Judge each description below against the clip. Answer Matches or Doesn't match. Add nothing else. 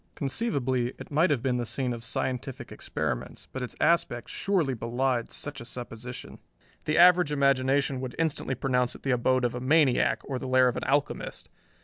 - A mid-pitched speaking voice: Doesn't match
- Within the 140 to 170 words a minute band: Doesn't match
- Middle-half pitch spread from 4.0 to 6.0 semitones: Doesn't match